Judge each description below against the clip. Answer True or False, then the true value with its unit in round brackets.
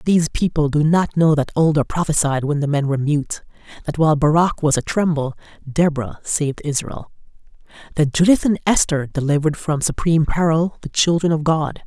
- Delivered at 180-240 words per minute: False (165 wpm)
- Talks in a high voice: False (155 Hz)